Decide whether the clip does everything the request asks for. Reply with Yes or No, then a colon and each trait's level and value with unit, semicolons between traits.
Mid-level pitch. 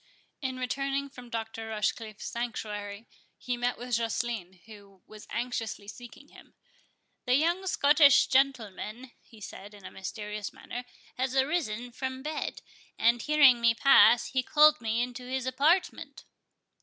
No: high, 245 Hz